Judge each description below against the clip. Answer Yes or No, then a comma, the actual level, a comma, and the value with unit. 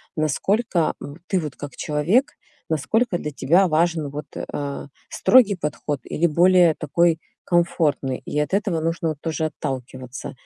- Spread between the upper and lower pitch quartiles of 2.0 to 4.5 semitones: Yes, average, 2.9 semitones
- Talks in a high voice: No, medium, 160 Hz